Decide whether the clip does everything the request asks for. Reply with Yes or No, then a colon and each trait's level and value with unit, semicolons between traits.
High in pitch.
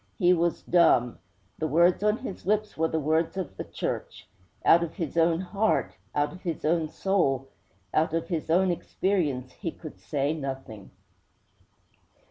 No: medium, 165 Hz